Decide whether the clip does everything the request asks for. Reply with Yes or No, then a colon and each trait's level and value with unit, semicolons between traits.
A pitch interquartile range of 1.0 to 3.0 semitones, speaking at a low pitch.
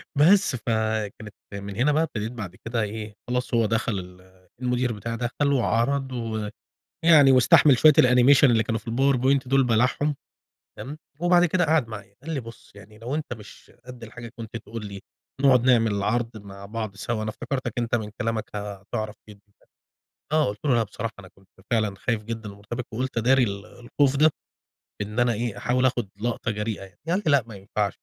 No: average, 3.6 semitones; low, 115 Hz